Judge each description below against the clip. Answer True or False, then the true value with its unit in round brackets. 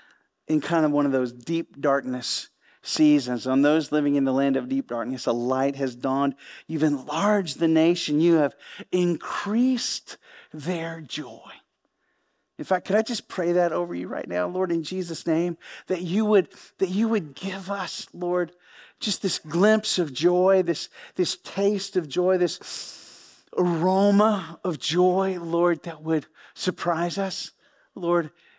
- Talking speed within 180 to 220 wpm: False (155 wpm)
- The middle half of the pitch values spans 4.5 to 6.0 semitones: False (4.0 semitones)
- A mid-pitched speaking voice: True (170 Hz)